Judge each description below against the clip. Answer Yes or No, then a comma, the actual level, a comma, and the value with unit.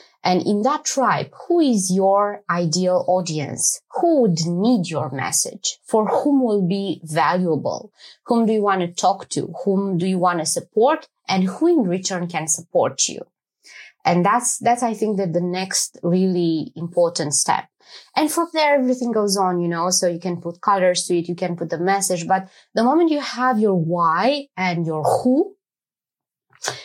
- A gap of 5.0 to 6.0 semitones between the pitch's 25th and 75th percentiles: Yes, wide, 5.5 semitones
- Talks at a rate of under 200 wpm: Yes, average, 180 wpm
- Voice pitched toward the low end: No, medium, 185 Hz